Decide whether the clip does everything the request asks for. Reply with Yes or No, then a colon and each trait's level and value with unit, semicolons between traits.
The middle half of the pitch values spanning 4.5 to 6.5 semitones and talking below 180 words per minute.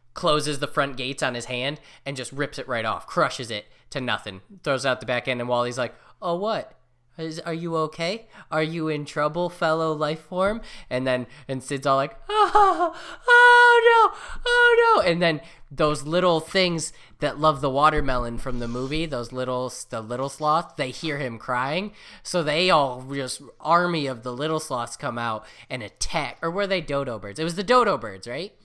No: average, 5.3 semitones; average, 200 wpm